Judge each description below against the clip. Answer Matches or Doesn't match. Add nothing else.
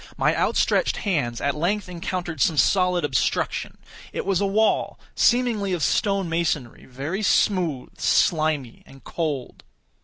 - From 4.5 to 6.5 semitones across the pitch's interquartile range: Matches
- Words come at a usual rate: Doesn't match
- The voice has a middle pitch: Matches